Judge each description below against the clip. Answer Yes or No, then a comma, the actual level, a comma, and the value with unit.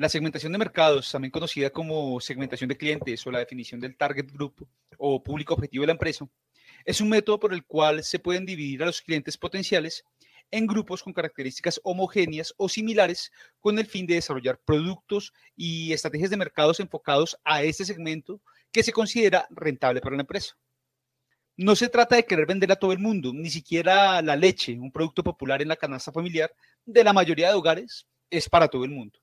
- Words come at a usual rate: No, fast, 195 wpm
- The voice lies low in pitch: No, medium, 160 Hz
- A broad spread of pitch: No, average, 5.0 semitones